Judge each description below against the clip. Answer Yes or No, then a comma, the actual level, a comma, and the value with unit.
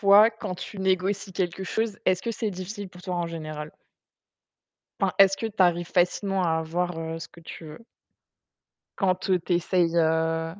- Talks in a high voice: No, medium, 180 Hz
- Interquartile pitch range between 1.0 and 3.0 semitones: Yes, narrow, 2.6 semitones